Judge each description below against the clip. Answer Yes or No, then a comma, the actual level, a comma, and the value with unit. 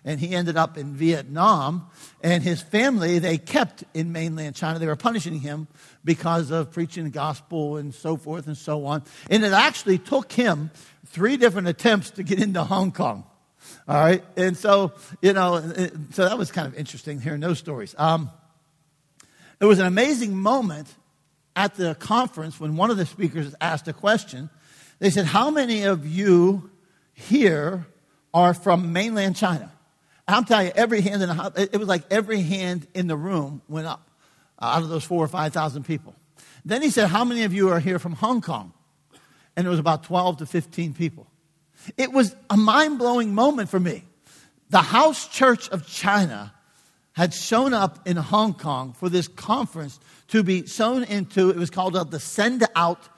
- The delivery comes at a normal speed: Yes, average, 185 wpm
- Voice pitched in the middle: Yes, medium, 175 Hz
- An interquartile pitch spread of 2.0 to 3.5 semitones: No, average, 4.3 semitones